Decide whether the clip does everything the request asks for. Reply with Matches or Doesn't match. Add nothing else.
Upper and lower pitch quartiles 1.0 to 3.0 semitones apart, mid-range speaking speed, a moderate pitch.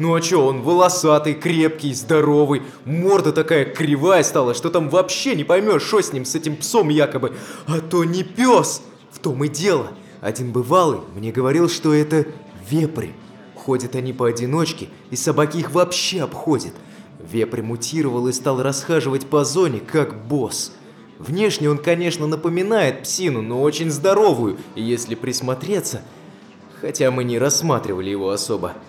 Doesn't match